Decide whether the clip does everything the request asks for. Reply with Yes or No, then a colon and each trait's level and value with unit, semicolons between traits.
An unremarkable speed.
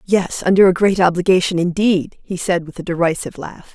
Yes: average, 190 wpm